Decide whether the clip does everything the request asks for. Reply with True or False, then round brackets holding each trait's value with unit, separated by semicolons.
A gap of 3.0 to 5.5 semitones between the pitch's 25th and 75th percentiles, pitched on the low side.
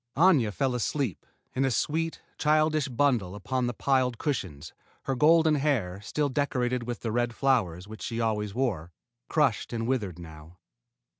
True (5.2 semitones; 125 Hz)